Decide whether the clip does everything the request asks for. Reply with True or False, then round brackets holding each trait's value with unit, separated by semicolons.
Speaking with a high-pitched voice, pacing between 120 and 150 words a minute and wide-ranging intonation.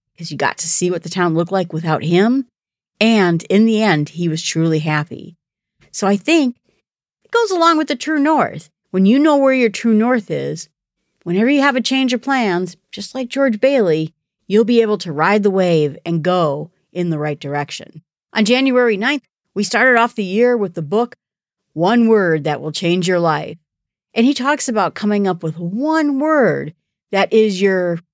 False (195 Hz; 195 wpm; 6.5 semitones)